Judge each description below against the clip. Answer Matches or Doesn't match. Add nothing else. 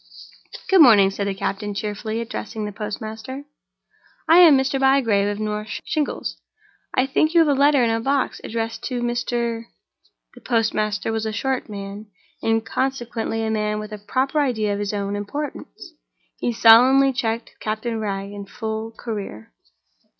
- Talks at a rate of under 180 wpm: Matches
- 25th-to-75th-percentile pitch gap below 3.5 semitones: Doesn't match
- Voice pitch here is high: Matches